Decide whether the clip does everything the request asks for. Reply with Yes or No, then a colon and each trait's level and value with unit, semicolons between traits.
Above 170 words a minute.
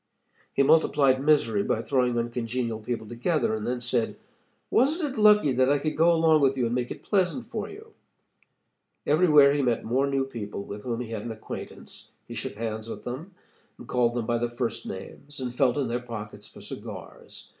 Yes: average, 200 wpm